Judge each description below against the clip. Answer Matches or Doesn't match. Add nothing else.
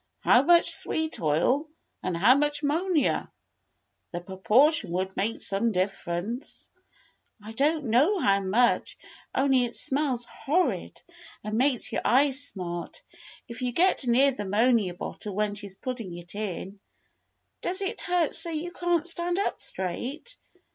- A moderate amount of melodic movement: Doesn't match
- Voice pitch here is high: Matches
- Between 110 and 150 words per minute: Matches